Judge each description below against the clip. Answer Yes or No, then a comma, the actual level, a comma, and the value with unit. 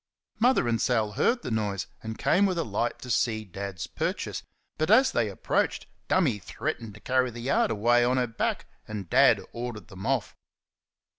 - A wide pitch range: No, average, 3.3 semitones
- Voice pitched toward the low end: Yes, low, 120 Hz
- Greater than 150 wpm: Yes, average, 180 wpm